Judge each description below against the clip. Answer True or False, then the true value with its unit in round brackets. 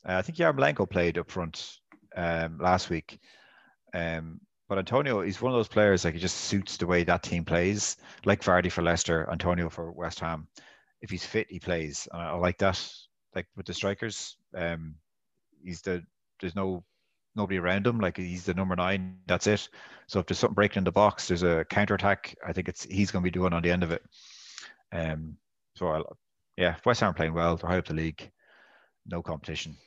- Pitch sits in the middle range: False (90 Hz)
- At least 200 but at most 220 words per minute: True (205 wpm)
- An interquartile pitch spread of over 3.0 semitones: False (2.5 semitones)